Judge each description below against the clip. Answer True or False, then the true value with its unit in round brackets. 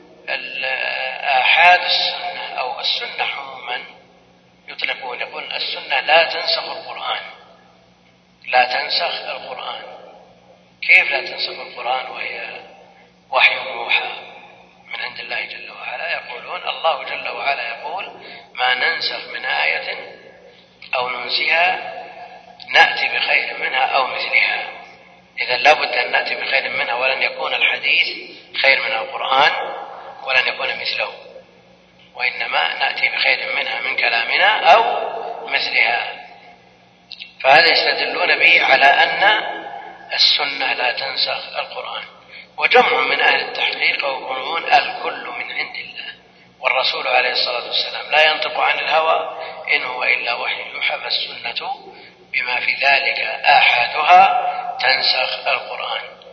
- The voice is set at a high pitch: True (365 Hz)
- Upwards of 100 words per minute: True (110 wpm)